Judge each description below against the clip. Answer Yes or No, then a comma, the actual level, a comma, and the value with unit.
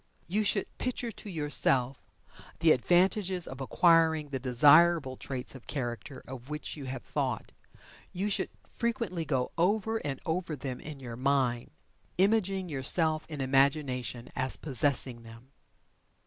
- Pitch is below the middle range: No, medium, 145 Hz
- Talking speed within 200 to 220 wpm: No, slow, 135 wpm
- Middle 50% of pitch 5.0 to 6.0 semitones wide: Yes, average, 5.3 semitones